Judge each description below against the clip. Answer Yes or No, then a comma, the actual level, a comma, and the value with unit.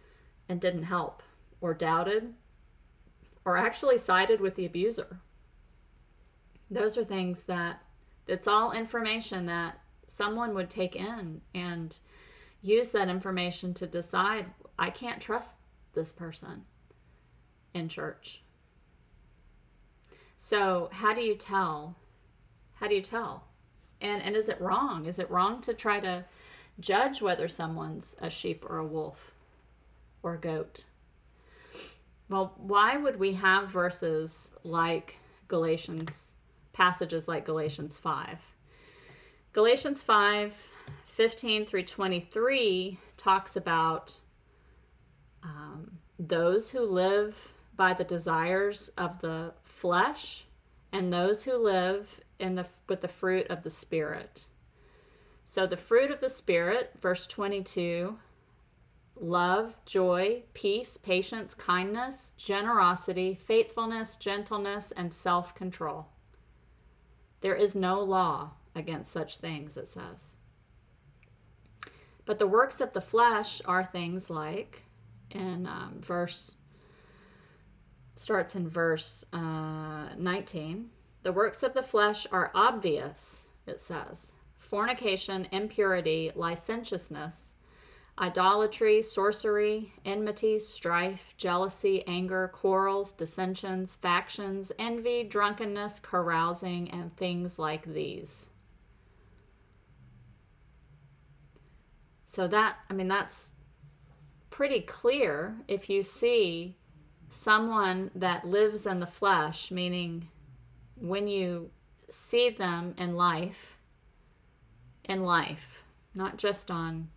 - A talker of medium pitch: Yes, medium, 180 Hz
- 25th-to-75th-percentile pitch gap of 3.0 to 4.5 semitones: Yes, average, 4.2 semitones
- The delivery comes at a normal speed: No, slow, 105 wpm